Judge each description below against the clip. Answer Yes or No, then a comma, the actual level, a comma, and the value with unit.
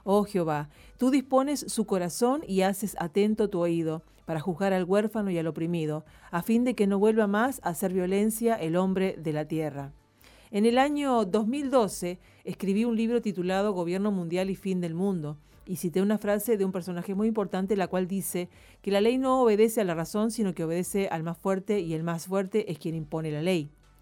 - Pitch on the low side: No, high, 190 Hz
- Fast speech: Yes, fast, 205 wpm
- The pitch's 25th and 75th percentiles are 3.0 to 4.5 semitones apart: Yes, average, 3.9 semitones